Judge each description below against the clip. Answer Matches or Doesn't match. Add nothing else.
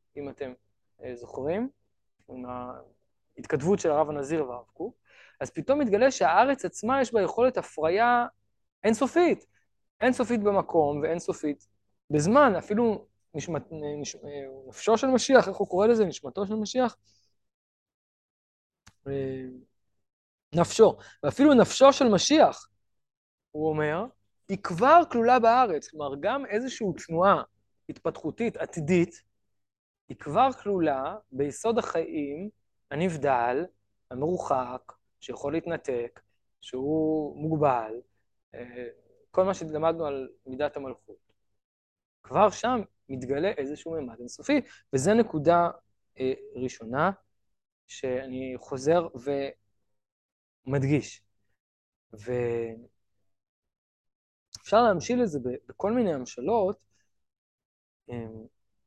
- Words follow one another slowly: Matches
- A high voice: Doesn't match